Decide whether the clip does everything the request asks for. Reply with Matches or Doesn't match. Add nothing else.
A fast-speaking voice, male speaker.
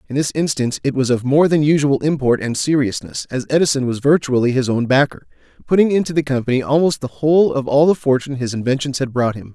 Matches